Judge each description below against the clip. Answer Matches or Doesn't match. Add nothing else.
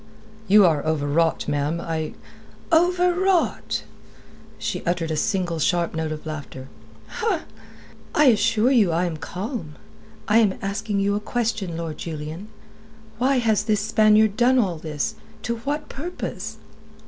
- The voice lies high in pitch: Matches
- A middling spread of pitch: Doesn't match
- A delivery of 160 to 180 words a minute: Doesn't match